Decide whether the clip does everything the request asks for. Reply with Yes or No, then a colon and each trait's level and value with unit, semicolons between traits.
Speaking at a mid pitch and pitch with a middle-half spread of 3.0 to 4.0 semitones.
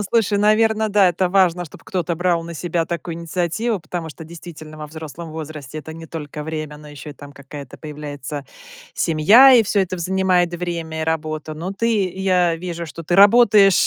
Yes: medium, 170 Hz; average, 3.5 semitones